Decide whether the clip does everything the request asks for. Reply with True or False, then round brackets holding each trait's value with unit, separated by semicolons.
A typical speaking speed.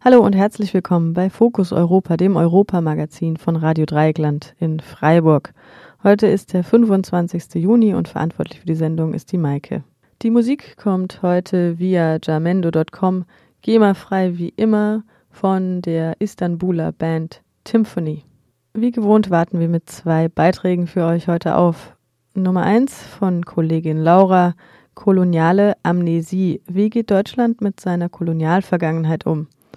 True (135 wpm)